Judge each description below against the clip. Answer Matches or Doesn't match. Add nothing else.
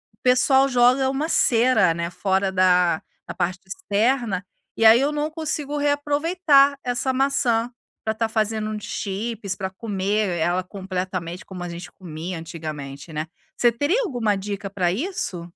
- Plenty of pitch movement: Matches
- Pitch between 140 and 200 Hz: Doesn't match